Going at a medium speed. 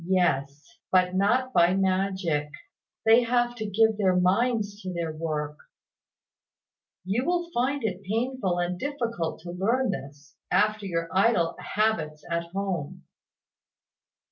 No: slow, 125 wpm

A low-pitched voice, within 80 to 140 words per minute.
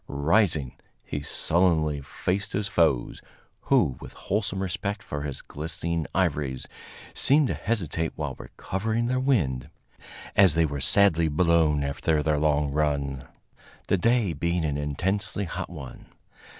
Yes: very low, 80 Hz; slow, 135 wpm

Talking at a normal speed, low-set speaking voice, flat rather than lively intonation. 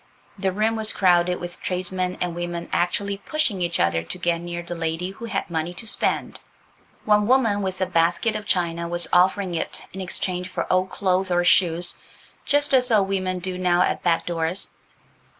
No: average, 185 wpm; medium, 180 Hz; narrow, 2.3 semitones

